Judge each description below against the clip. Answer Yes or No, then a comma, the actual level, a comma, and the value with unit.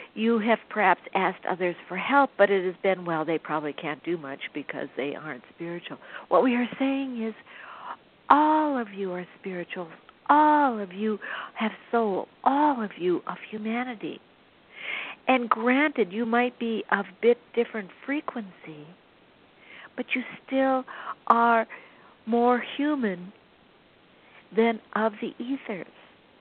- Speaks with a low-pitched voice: No, high, 225 Hz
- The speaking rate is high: No, average, 140 wpm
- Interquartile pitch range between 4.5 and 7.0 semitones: Yes, average, 5.0 semitones